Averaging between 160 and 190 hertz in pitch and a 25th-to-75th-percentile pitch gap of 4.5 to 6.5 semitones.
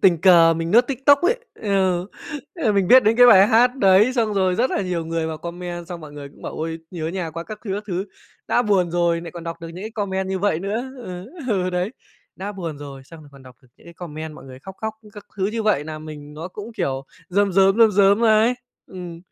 No: medium, 185 Hz; average, 4.0 semitones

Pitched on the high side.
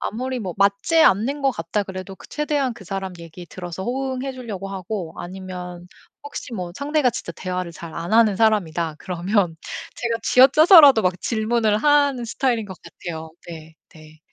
Yes: high, 200 Hz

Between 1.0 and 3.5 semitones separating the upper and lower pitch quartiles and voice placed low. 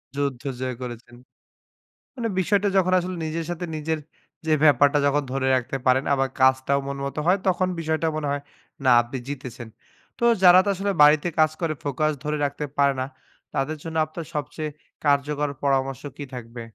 No: average, 3.0 semitones; medium, 145 Hz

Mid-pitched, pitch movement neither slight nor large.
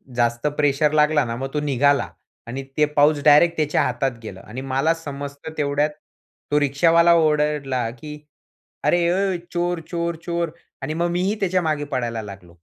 Yes: medium, 150 Hz; average, 3.5 semitones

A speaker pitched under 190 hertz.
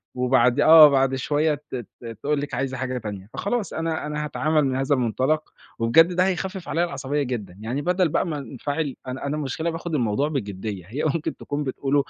Yes: medium, 140 Hz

